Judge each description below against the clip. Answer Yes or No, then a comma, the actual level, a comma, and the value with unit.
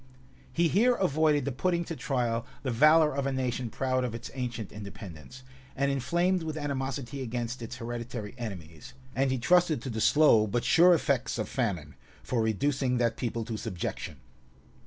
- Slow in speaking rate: No, average, 170 wpm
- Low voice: Yes, low, 130 Hz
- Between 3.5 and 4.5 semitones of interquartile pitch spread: Yes, average, 4.1 semitones